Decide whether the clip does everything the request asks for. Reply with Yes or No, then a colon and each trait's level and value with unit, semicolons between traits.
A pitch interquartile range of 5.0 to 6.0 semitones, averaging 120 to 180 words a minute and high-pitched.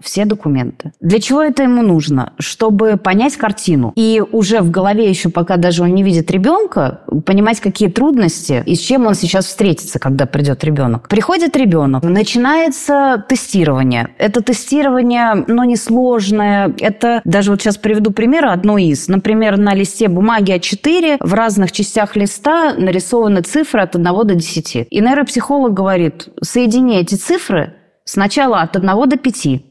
Yes: average, 5.3 semitones; average, 155 wpm; high, 205 Hz